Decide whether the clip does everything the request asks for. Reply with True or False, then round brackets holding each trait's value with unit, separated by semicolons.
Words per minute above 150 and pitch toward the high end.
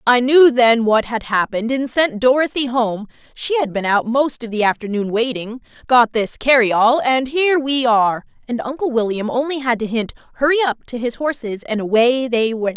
True (190 wpm; 245 Hz)